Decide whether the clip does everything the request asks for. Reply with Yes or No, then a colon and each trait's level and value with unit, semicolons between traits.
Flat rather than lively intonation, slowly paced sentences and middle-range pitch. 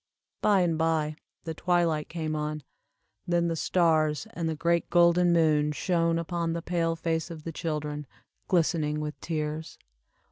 No: narrow, 1.9 semitones; average, 150 wpm; medium, 165 Hz